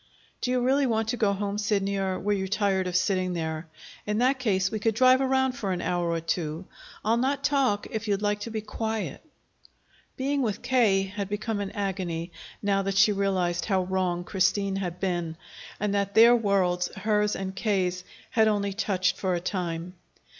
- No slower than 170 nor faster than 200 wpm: Yes, average, 190 wpm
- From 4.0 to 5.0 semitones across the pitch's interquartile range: No, average, 3.0 semitones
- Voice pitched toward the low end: No, high, 200 Hz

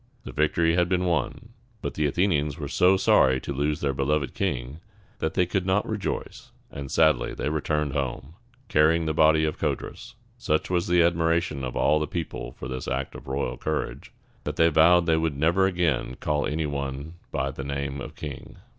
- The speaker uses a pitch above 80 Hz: No, very low, 75 Hz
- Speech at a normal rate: Yes, average, 190 wpm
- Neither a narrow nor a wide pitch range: Yes, average, 3.2 semitones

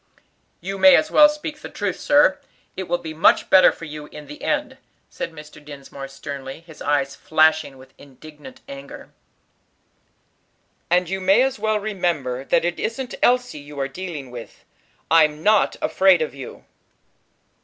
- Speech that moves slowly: No, average, 160 wpm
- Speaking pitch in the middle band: Yes, medium, 160 Hz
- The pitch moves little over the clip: No, average, 5.3 semitones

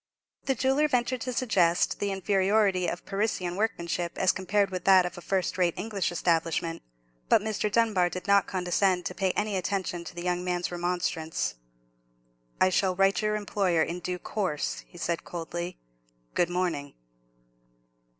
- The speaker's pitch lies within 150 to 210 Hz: Yes, medium, 185 Hz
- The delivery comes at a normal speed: Yes, average, 160 wpm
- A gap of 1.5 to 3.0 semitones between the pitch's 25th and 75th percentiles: Yes, narrow, 2.6 semitones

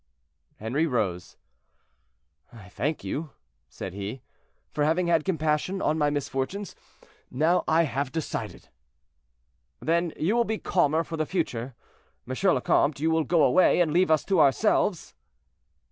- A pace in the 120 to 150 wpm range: Yes, average, 145 wpm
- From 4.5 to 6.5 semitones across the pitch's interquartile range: No, average, 4.1 semitones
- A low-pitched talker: No, medium, 155 Hz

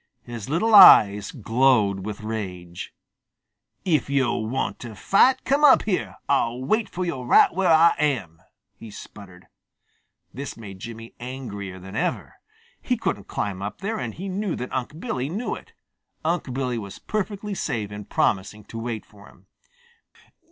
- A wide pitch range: Yes, wide, 8.4 semitones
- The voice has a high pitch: No, low, 120 Hz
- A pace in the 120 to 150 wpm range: No, average, 160 wpm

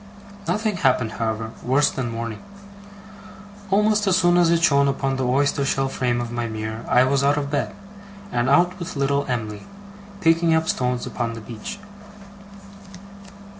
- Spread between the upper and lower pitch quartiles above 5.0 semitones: Yes, wide, 5.4 semitones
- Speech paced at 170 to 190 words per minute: No, average, 160 wpm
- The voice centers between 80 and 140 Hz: Yes, low, 135 Hz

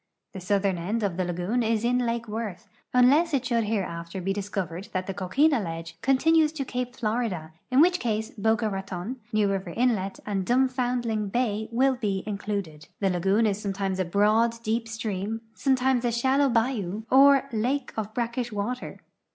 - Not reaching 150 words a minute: No, average, 175 wpm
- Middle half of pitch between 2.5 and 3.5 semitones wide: No, average, 4.1 semitones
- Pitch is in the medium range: No, high, 220 Hz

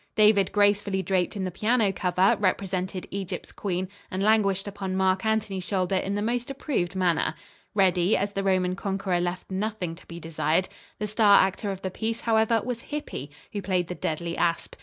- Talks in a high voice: Yes, high, 195 Hz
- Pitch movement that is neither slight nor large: No, narrow, 2.3 semitones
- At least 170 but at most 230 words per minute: Yes, average, 180 wpm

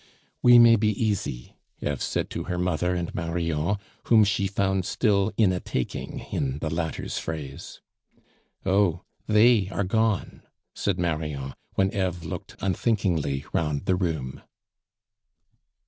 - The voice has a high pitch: No, very low, 90 Hz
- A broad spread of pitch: No, average, 4.3 semitones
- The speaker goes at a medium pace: No, slow, 130 wpm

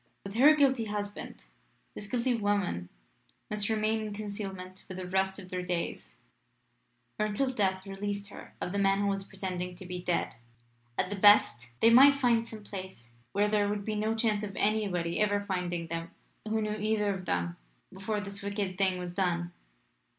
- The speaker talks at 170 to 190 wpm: Yes, average, 180 wpm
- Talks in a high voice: Yes, high, 200 Hz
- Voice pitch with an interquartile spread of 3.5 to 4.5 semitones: No, narrow, 2.6 semitones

